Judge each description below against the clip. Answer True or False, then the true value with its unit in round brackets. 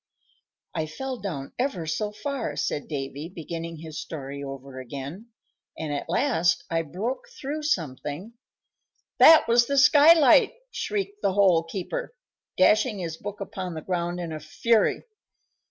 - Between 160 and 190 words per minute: False (140 wpm)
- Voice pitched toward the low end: False (180 Hz)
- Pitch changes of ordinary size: False (7.6 semitones)